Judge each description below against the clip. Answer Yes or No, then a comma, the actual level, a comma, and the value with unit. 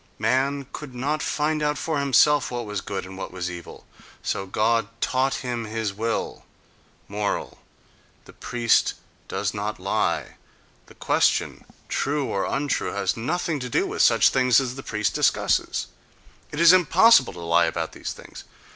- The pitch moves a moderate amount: No, wide, 5.8 semitones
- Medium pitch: No, low, 125 Hz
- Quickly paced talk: No, average, 155 wpm